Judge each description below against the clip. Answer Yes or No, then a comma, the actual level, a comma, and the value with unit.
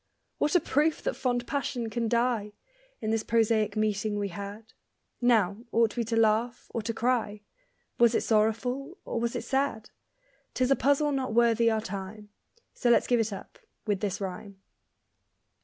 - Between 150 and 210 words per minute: Yes, average, 170 wpm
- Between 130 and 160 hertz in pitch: No, high, 225 Hz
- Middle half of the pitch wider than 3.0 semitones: No, narrow, 2.5 semitones